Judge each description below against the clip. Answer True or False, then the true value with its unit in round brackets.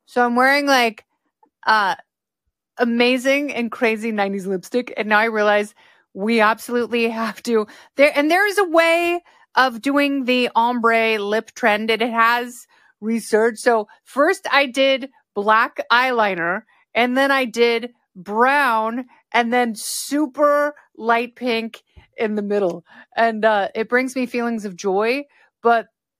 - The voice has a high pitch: True (235 Hz)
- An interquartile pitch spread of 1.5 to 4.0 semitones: True (3.4 semitones)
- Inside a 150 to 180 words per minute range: False (140 wpm)